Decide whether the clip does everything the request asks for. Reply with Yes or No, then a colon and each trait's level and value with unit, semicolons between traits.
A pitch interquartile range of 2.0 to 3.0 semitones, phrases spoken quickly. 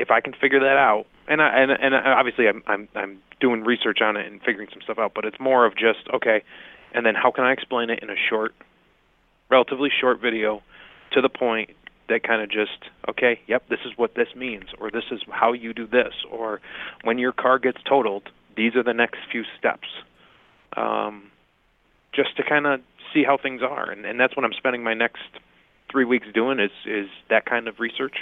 Yes: average, 2.7 semitones; fast, 215 wpm